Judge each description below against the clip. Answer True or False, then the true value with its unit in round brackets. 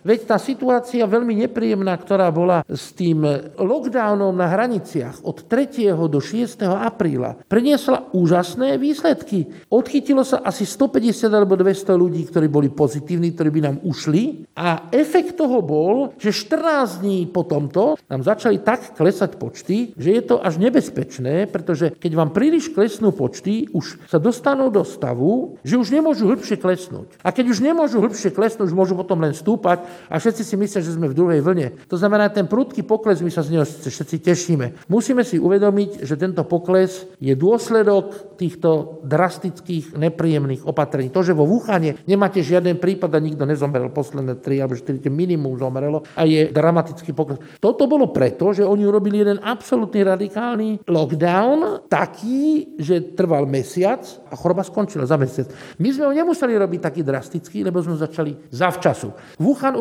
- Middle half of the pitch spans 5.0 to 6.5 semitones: True (5.4 semitones)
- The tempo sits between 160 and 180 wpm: True (165 wpm)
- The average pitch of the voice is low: False (185 Hz)